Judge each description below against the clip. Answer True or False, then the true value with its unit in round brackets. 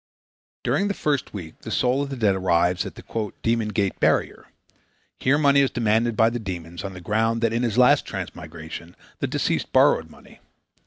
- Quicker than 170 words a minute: True (190 wpm)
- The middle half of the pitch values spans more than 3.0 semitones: True (4.6 semitones)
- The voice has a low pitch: True (110 Hz)